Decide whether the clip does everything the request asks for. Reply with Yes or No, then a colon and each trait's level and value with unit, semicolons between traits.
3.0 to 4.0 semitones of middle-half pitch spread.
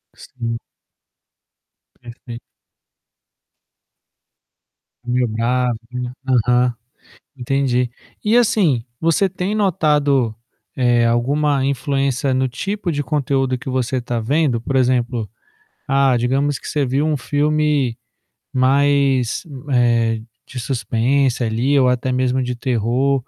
No: narrow, 2.6 semitones